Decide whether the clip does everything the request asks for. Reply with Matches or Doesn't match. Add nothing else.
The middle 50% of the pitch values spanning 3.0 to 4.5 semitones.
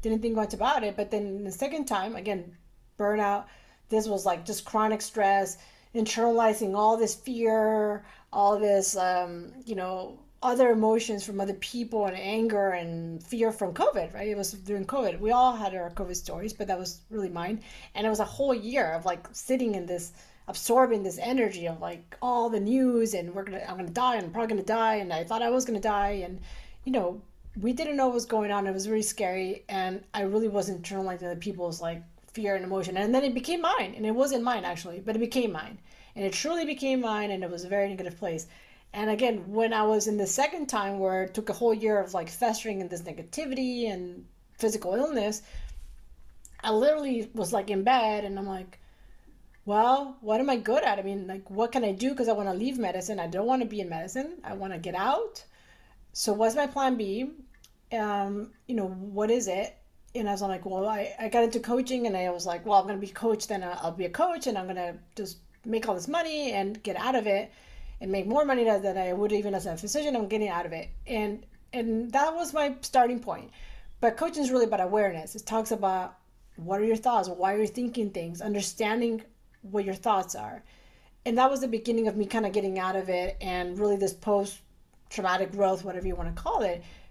Matches